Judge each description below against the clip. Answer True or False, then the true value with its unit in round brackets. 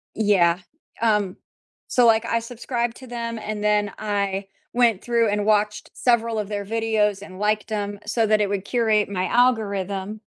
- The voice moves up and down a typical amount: False (2.2 semitones)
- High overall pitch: True (210 Hz)